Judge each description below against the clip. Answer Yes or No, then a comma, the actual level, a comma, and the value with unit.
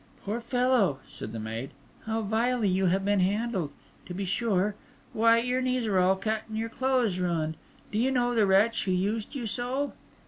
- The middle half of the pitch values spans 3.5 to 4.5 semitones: Yes, average, 4.2 semitones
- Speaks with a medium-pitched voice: No, high, 215 Hz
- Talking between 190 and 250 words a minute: Yes, average, 195 wpm